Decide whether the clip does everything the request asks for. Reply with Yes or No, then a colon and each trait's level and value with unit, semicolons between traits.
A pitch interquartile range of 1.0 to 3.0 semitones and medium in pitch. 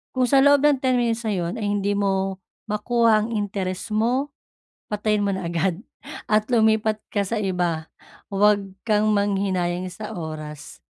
No: average, 2.7 semitones; high, 205 Hz